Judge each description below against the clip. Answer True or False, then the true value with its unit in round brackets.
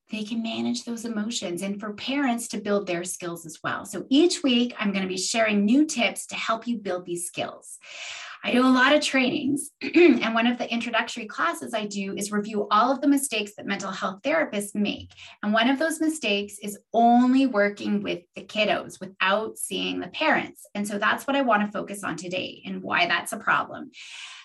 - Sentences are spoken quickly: True (210 wpm)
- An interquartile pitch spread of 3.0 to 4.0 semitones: False (4.5 semitones)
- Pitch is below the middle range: False (215 Hz)